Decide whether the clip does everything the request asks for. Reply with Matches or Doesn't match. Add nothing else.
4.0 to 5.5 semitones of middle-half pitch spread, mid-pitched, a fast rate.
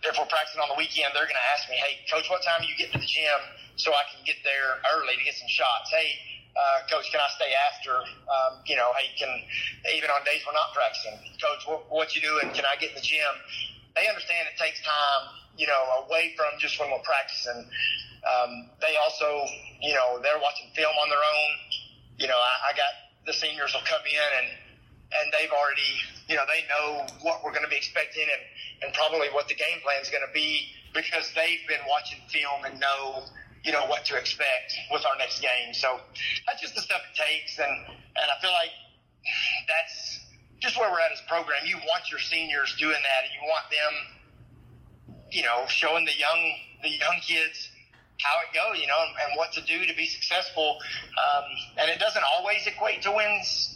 Doesn't match